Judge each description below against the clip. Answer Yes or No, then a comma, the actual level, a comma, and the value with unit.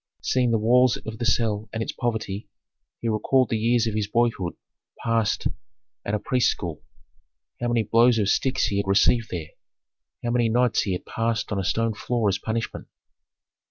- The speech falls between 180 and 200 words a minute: Yes, average, 185 wpm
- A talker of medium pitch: No, low, 115 Hz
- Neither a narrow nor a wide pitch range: No, narrow, 2.3 semitones